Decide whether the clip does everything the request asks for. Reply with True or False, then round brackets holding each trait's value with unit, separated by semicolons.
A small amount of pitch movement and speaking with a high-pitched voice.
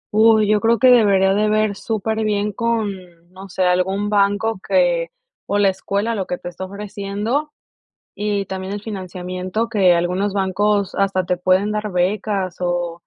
True (2.3 semitones; 200 Hz)